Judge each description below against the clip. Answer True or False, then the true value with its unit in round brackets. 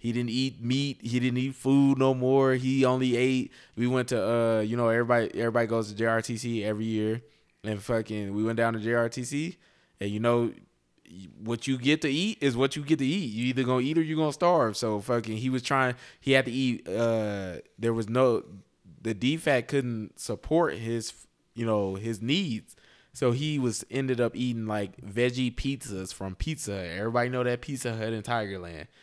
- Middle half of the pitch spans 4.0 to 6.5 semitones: False (2.8 semitones)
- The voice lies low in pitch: True (120 Hz)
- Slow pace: False (195 wpm)